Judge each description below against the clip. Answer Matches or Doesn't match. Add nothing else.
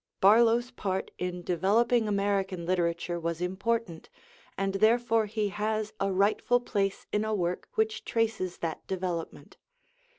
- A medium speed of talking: Doesn't match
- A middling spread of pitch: Matches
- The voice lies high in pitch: Matches